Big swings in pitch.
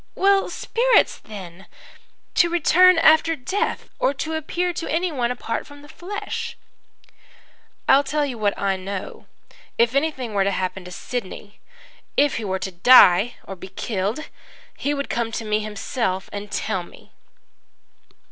Yes: wide, 7.9 semitones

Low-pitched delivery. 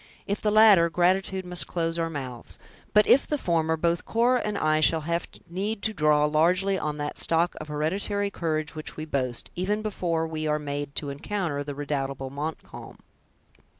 No: medium, 165 Hz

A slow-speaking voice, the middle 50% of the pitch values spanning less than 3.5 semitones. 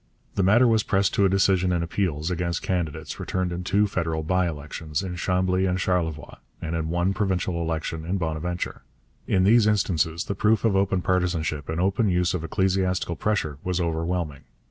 No: average, 180 wpm; average, 2.8 semitones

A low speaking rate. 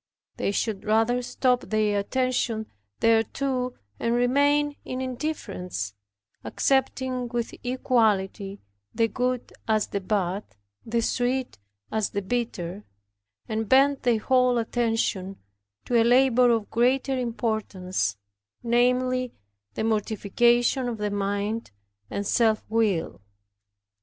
Yes: slow, 110 wpm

